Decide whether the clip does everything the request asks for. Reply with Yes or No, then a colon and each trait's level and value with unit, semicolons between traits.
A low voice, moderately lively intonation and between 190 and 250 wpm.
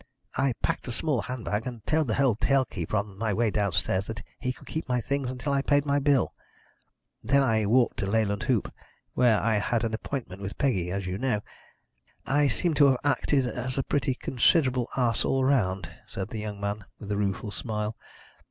Yes: low, 115 Hz; average, 4.4 semitones; average, 200 wpm